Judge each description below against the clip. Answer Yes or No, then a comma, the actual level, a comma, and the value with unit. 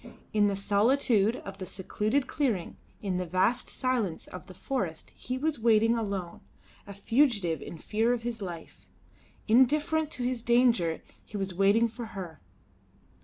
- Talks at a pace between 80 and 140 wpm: No, average, 155 wpm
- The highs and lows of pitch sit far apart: No, average, 4.3 semitones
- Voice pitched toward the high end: Yes, high, 220 Hz